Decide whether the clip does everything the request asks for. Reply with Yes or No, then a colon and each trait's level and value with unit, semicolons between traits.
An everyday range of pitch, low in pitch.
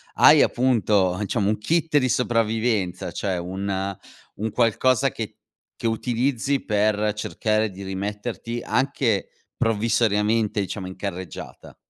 Yes: average, 3.0 semitones; low, 105 Hz